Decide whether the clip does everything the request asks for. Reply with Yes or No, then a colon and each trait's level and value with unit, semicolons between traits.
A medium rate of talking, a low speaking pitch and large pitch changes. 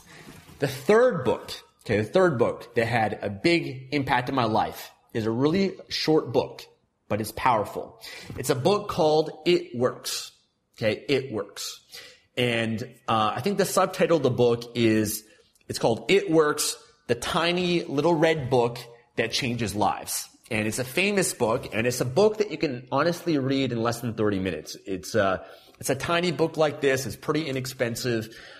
No: average, 175 wpm; medium, 145 Hz; wide, 6.5 semitones